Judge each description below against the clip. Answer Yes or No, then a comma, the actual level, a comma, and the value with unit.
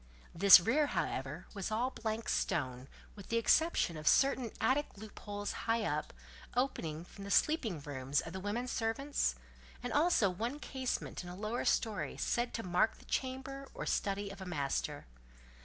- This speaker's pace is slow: No, average, 165 wpm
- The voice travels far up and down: Yes, wide, 5.9 semitones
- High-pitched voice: Yes, high, 215 Hz